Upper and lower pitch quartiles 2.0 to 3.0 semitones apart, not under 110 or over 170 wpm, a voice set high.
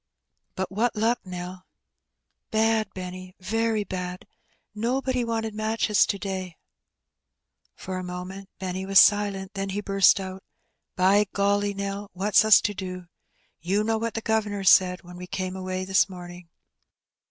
Yes: narrow, 2.5 semitones; average, 155 wpm; high, 195 Hz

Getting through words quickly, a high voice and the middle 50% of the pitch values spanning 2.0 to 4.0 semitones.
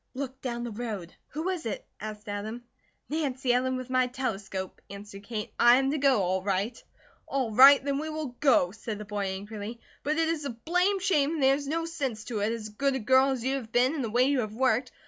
No: fast, 235 wpm; very high, 250 Hz; average, 4.6 semitones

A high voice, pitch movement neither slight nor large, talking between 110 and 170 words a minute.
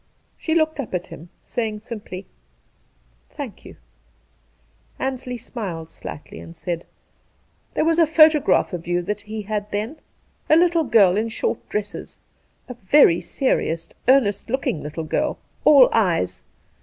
No: high, 215 Hz; wide, 7.1 semitones; average, 150 wpm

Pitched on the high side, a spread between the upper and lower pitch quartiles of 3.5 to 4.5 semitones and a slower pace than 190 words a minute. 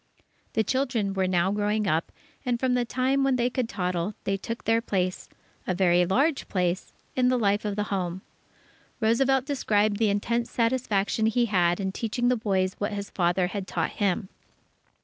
Yes: high, 210 Hz; average, 4.1 semitones; average, 180 wpm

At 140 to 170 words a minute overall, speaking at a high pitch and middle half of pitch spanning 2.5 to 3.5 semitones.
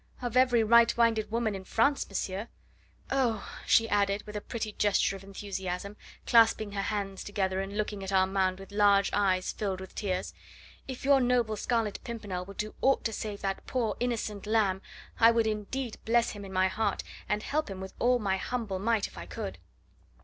No: average, 190 wpm; high, 210 Hz; average, 2.9 semitones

